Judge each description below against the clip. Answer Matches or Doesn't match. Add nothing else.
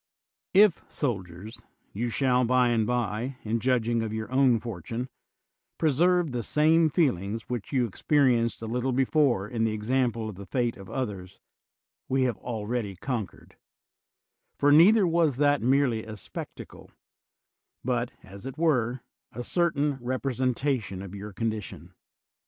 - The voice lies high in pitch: Doesn't match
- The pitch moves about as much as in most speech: Matches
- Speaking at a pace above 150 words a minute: Doesn't match